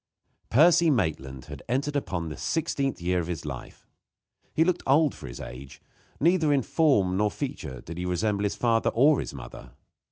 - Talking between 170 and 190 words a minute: Yes, average, 185 wpm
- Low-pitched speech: Yes, low, 115 Hz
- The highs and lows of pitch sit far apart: Yes, wide, 9.0 semitones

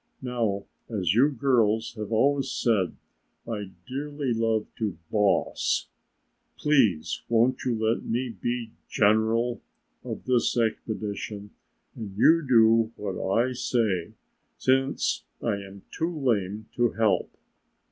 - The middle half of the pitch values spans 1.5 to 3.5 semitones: Yes, average, 3.2 semitones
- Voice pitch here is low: Yes, low, 115 Hz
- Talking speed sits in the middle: No, slow, 115 wpm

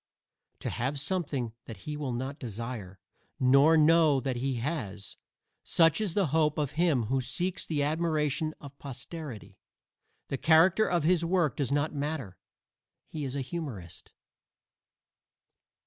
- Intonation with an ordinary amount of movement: Yes, average, 4.0 semitones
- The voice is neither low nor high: Yes, medium, 145 Hz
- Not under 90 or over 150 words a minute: Yes, average, 140 wpm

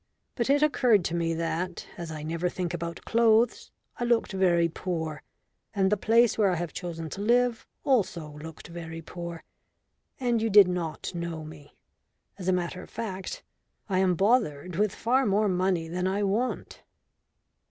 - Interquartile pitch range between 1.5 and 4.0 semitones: No, average, 4.4 semitones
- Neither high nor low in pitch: Yes, medium, 180 Hz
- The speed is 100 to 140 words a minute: No, average, 175 wpm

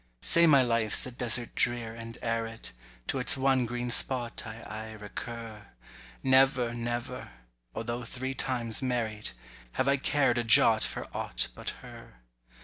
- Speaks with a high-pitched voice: No, low, 120 Hz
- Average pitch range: No, narrow, 2.2 semitones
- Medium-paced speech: Yes, average, 145 wpm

